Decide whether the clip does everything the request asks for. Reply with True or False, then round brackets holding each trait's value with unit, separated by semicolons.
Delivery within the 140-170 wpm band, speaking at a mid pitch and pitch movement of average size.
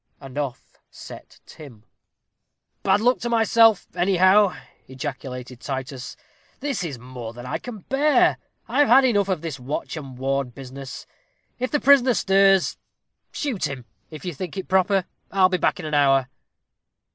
False (150 wpm; 170 Hz; 7.6 semitones)